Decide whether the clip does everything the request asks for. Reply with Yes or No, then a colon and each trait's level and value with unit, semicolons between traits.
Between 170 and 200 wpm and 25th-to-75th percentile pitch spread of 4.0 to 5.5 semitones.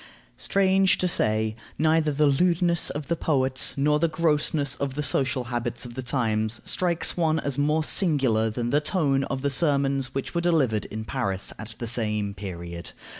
Yes: average, 175 wpm; average, 5.1 semitones